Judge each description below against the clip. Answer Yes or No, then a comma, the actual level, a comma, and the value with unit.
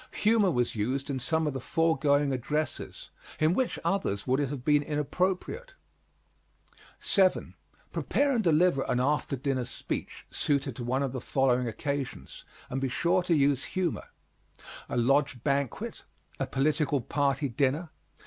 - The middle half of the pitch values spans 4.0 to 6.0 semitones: No, average, 3.5 semitones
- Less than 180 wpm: Yes, average, 150 wpm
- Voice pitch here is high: No, medium, 140 Hz